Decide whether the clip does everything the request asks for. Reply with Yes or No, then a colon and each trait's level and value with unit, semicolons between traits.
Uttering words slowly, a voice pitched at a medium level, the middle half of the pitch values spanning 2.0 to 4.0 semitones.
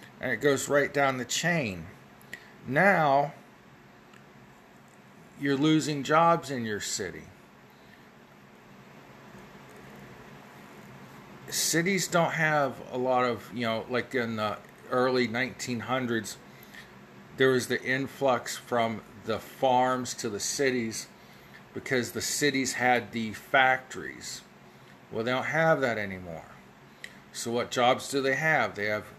No: slow, 115 wpm; low, 125 Hz; average, 3.3 semitones